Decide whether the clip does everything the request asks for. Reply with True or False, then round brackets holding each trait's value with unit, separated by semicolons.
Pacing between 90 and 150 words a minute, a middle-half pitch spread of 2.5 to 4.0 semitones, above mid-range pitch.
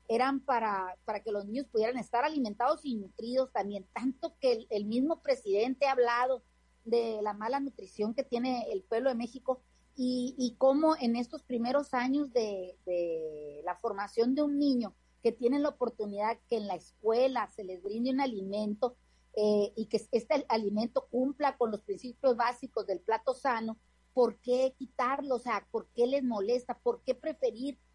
False (175 wpm; 3.3 semitones; 240 Hz)